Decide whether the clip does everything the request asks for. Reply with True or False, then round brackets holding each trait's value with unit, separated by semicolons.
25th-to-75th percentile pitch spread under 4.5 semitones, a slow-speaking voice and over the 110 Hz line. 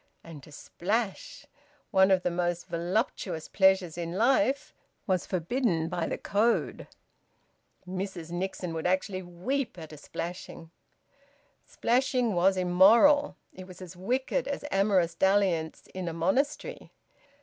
True (3.9 semitones; 125 wpm; 185 Hz)